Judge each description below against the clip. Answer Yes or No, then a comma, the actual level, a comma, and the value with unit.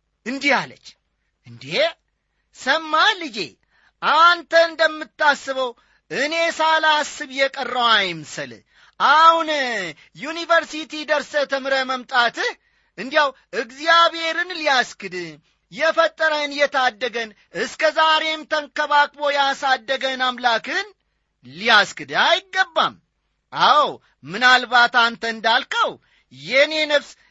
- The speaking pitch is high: Yes, very high, 290 Hz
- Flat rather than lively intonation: No, average, 4.2 semitones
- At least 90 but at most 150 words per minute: No, average, 75 wpm